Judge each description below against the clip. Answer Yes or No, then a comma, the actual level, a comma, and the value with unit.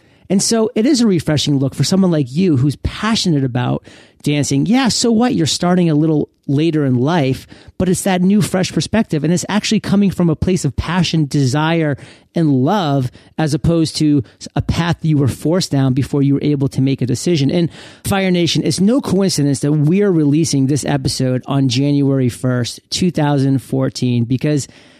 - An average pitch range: Yes, average, 4.7 semitones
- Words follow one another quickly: No, average, 180 wpm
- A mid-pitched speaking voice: Yes, medium, 150 Hz